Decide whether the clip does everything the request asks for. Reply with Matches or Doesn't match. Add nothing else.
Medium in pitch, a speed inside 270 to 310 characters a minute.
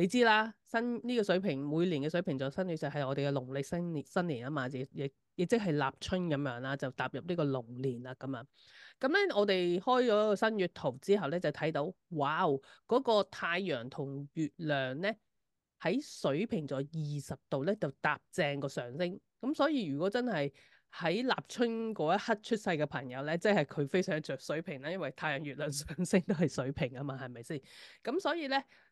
Matches